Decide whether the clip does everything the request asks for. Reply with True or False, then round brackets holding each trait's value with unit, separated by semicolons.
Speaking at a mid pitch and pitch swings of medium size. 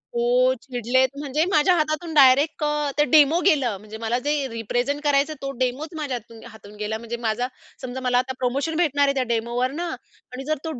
False (260 Hz; 3.6 semitones)